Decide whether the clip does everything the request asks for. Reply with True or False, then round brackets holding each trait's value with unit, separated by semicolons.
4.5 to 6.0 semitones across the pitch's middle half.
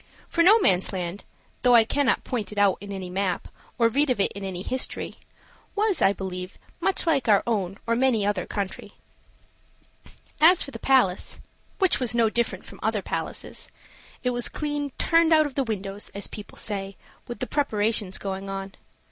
True (5.6 semitones)